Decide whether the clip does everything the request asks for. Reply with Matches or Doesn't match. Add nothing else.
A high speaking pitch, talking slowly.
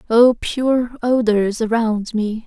Matches